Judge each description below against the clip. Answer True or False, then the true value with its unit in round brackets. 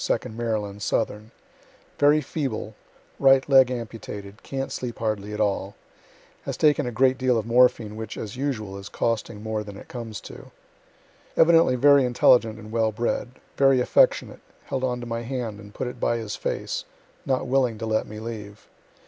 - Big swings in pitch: False (3.2 semitones)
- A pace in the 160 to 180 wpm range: True (175 wpm)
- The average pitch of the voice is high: False (115 Hz)